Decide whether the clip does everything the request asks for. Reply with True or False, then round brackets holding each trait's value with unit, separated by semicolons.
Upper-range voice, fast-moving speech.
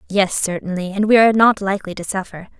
True (195 Hz; 210 wpm)